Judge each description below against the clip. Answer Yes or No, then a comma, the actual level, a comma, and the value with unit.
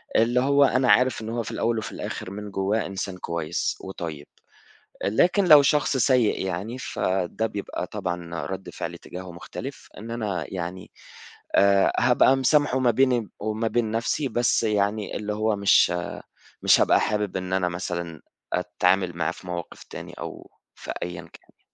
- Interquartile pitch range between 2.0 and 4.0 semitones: No, average, 4.7 semitones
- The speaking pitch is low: Yes, low, 105 Hz